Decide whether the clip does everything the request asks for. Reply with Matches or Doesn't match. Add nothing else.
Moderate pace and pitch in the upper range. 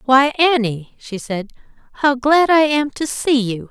Matches